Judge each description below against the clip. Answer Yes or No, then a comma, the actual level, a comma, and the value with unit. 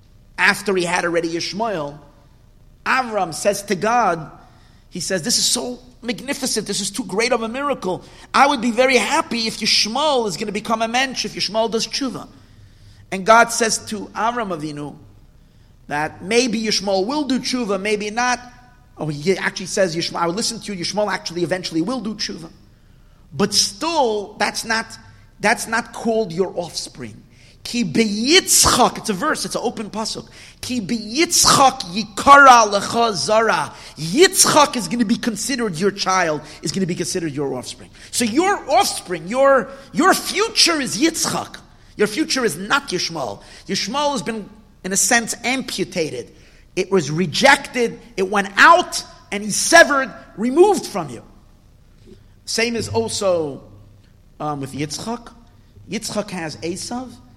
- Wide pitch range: Yes, wide, 5.9 semitones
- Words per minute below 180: Yes, average, 155 wpm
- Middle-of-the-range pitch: No, high, 210 Hz